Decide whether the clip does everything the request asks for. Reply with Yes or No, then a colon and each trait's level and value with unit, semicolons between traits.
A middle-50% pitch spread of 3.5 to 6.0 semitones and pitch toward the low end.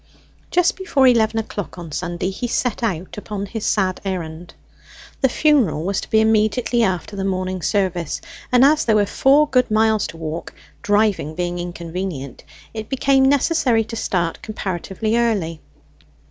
No: average, 4.8 semitones; high, 205 Hz